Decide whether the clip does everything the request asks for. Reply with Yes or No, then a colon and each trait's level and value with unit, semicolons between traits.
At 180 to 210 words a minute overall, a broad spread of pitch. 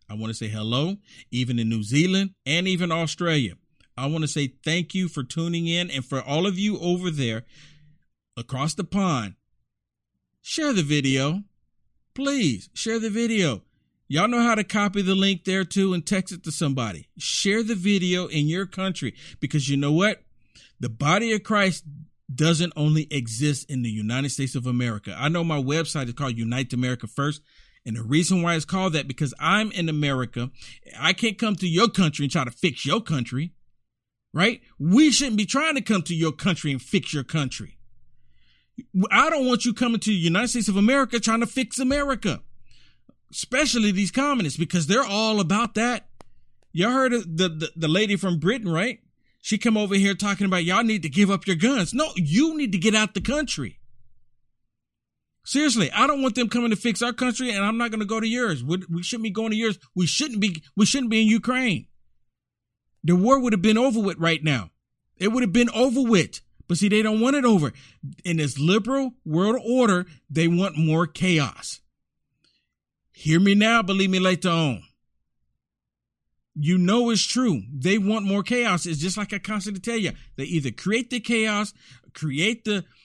Yes: average, 195 wpm; wide, 7.2 semitones